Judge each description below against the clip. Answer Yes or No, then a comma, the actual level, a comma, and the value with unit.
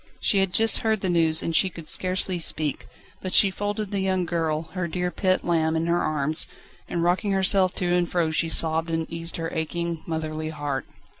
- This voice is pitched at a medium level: Yes, medium, 170 Hz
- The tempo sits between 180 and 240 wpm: Yes, fast, 205 wpm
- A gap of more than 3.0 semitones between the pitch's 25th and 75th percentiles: No, narrow, 2.6 semitones